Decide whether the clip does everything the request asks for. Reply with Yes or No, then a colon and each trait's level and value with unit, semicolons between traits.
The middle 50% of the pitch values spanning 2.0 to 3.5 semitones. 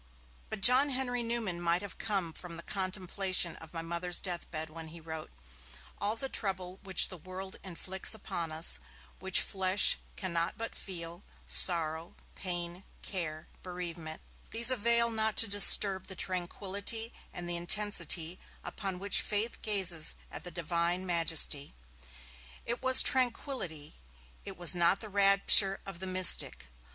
Yes: average, 3.2 semitones